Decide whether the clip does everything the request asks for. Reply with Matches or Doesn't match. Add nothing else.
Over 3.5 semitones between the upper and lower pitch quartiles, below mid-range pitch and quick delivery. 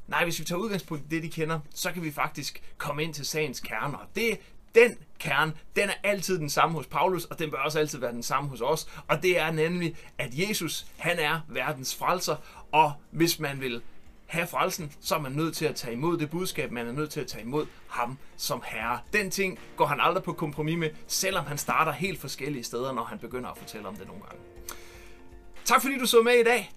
Doesn't match